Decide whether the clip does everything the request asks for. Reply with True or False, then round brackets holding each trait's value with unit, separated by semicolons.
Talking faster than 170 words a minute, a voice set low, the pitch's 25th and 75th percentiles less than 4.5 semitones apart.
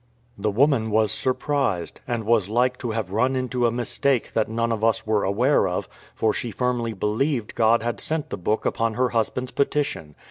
True (190 wpm; 115 Hz; 2.7 semitones)